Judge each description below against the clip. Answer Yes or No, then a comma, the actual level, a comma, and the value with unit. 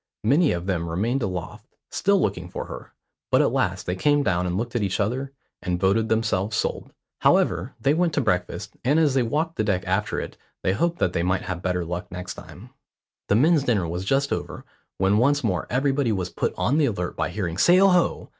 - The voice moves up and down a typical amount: No, wide, 7.2 semitones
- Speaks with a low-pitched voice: Yes, low, 105 Hz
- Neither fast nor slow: No, fast, 215 wpm